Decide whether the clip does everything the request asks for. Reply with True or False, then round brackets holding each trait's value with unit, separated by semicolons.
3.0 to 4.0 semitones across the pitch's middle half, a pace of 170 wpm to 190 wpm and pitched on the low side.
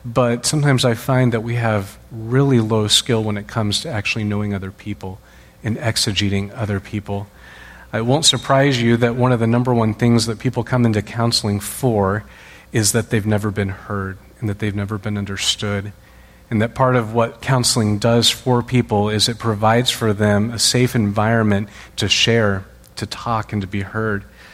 False (2.5 semitones; 185 wpm; 110 Hz)